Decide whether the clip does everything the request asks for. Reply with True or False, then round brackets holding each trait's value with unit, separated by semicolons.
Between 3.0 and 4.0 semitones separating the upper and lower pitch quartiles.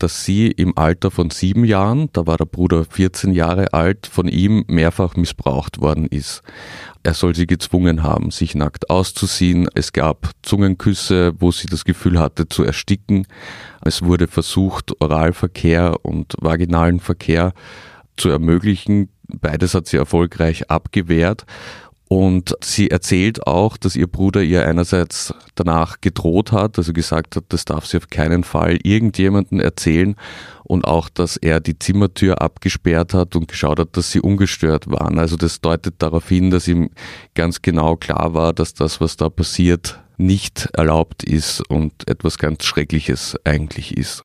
False (2.6 semitones)